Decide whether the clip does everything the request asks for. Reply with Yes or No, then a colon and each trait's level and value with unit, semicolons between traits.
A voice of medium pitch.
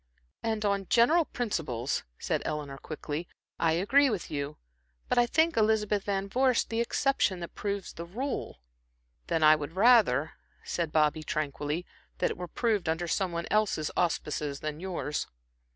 Yes: medium, 180 Hz